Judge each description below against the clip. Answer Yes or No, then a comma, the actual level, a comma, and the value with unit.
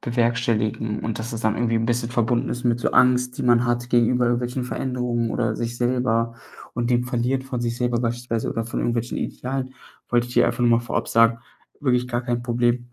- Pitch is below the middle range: Yes, low, 120 Hz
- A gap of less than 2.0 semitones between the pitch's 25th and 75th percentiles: Yes, narrow, 1.0 semitones